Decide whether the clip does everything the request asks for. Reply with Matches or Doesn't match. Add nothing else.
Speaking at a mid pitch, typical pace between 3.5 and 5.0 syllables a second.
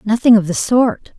Doesn't match